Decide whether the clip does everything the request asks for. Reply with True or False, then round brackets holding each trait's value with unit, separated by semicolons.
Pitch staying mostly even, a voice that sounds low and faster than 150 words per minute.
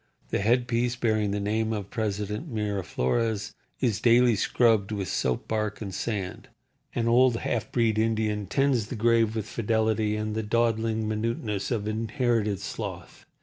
False (1.9 semitones; 110 Hz; 145 wpm)